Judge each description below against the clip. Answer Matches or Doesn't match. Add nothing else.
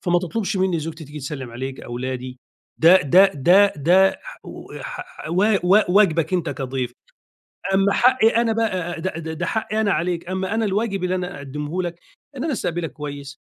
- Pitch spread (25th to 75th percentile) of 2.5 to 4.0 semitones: Doesn't match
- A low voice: Doesn't match